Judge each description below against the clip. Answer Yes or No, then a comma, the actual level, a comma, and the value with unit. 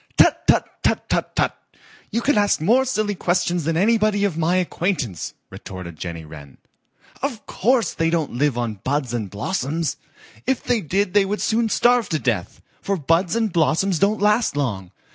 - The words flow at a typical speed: Yes, average, 175 wpm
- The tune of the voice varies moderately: No, wide, 7.7 semitones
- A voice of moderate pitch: Yes, medium, 175 Hz